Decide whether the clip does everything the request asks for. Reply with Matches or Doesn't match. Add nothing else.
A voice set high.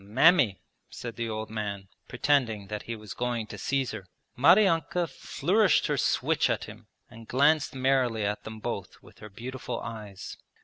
Doesn't match